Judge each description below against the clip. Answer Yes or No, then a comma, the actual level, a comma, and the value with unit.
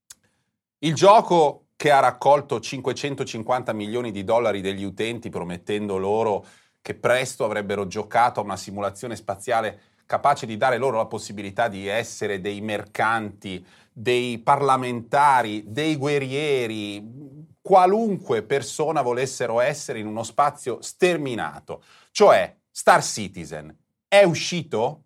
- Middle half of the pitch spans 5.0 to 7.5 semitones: Yes, wide, 5.5 semitones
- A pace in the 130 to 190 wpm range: No, slow, 115 wpm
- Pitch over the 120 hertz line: No, low, 115 Hz